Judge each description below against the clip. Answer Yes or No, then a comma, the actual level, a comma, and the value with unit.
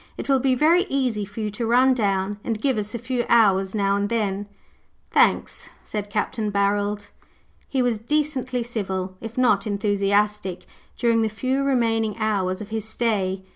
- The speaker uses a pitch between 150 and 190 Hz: No, high, 215 Hz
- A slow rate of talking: No, average, 175 wpm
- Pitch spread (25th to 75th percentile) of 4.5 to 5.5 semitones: No, average, 3.1 semitones